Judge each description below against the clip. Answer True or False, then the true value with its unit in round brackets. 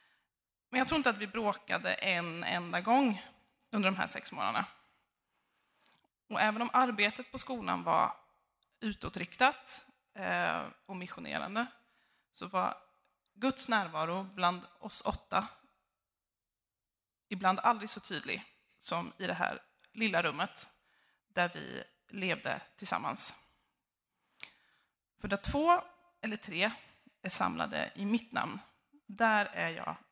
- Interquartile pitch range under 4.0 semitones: False (5.0 semitones)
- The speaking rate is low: True (120 wpm)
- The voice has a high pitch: True (220 Hz)